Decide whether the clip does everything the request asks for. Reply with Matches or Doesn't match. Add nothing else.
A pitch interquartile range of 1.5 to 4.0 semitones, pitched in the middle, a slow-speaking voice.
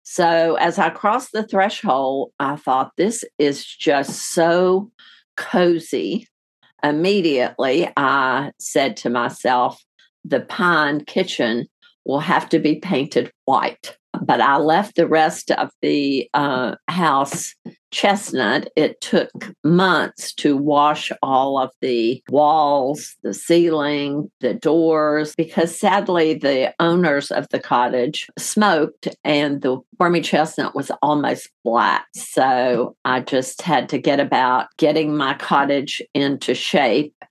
Matches